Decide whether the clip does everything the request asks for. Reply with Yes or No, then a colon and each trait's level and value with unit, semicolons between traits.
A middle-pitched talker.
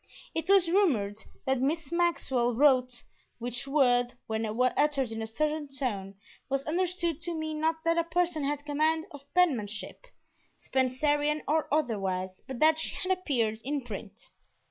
No: very high, 285 Hz